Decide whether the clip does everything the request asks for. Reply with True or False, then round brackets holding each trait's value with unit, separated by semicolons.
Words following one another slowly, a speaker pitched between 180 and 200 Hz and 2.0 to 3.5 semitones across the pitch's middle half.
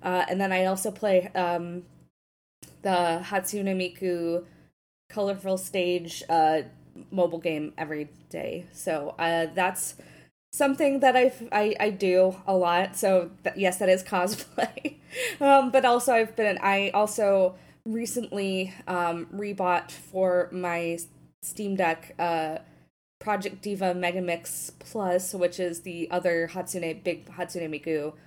True (130 wpm; 185 Hz; 2.9 semitones)